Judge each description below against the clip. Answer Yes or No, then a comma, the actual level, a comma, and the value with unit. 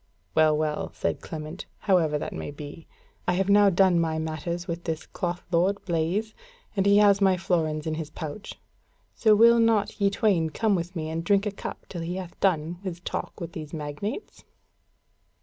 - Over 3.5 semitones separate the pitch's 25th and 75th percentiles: Yes, average, 3.9 semitones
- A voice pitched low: No, medium, 175 Hz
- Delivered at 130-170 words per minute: No, average, 185 wpm